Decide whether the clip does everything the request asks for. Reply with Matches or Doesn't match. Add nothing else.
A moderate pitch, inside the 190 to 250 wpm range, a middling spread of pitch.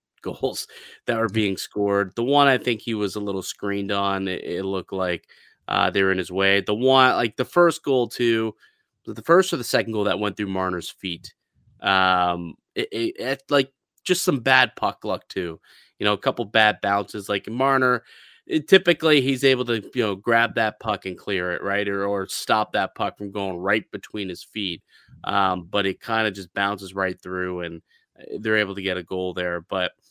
Doesn't match